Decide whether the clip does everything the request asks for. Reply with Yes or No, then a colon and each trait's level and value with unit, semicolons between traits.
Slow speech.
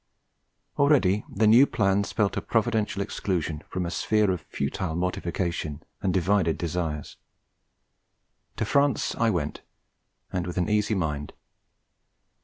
Yes: slow, 125 wpm